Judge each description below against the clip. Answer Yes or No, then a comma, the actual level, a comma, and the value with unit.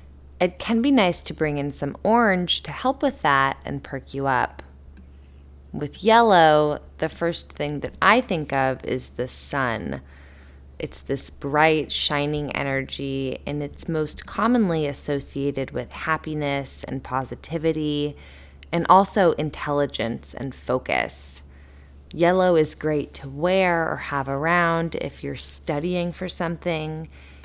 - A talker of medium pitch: Yes, medium, 145 Hz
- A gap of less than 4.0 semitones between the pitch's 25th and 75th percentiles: No, average, 4.3 semitones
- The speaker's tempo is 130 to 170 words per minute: Yes, slow, 135 wpm